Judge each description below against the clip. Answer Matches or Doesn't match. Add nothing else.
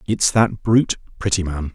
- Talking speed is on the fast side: Doesn't match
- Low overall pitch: Matches